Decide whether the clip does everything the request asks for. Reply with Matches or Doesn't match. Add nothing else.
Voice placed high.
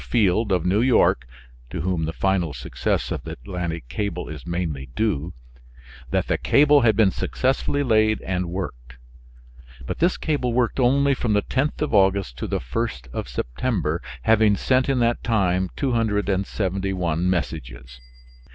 Doesn't match